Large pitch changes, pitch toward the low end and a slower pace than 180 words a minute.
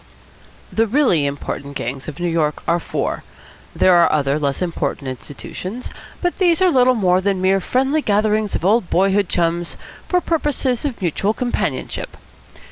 No: wide, 7.0 semitones; high, 190 Hz; average, 155 wpm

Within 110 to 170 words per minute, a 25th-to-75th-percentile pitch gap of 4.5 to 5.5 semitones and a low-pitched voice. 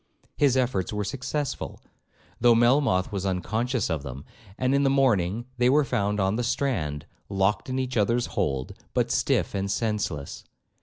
Yes: average, 160 wpm; average, 5.2 semitones; low, 110 Hz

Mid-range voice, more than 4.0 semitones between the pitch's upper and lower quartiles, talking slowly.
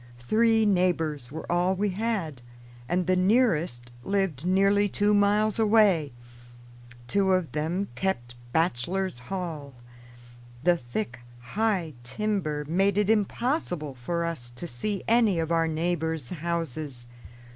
Yes: medium, 175 Hz; average, 5.1 semitones; slow, 125 wpm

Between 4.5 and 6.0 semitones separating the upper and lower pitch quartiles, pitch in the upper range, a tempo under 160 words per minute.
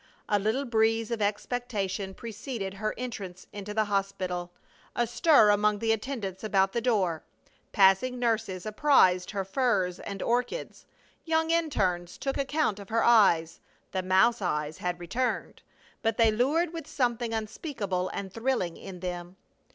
No: average, 4.1 semitones; high, 210 Hz; average, 145 wpm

